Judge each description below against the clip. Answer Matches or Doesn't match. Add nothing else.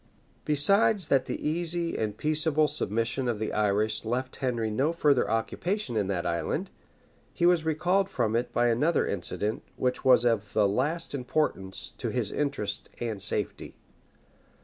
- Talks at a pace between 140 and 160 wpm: Matches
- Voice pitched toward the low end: Matches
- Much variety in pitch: Matches